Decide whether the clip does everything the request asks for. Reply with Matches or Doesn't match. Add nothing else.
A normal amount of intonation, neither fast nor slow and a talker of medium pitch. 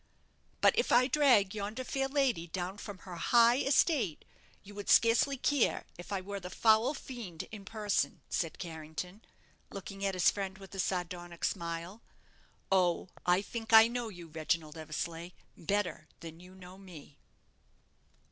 Doesn't match